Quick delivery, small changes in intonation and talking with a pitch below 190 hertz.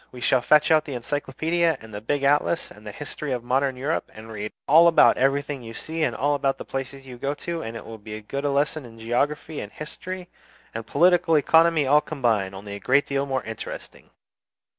No: fast, 220 wpm; average, 4.7 semitones; medium, 140 Hz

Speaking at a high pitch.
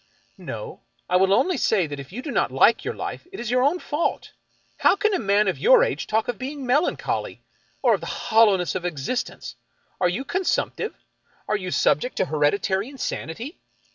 Yes: high, 220 Hz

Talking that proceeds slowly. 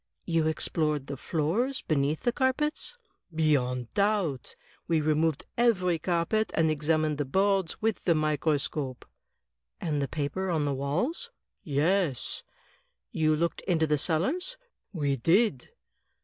Yes: slow, 125 wpm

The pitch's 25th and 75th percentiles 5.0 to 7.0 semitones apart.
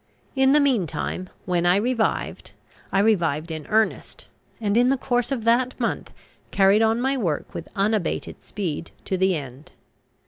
Yes: wide, 5.6 semitones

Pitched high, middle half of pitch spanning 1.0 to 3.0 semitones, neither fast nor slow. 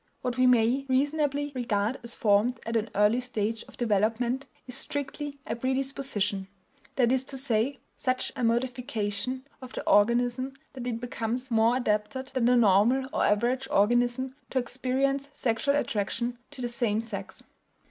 Yes: high, 245 Hz; average, 2.7 semitones; average, 155 wpm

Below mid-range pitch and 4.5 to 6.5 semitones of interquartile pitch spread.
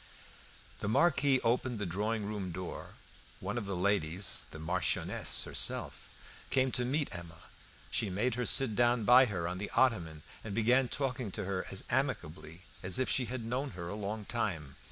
Yes: low, 105 Hz; average, 5.2 semitones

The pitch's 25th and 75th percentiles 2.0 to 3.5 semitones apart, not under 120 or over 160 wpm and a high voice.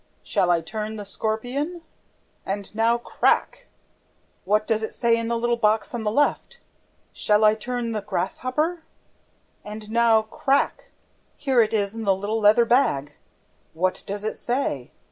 Yes: narrow, 2.4 semitones; average, 155 wpm; high, 220 Hz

